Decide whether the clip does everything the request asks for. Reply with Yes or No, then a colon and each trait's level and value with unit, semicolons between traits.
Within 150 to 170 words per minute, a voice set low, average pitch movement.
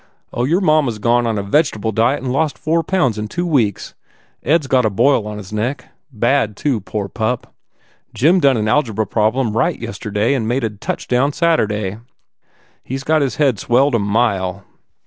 No: average, 195 wpm; low, 120 Hz; average, 4.7 semitones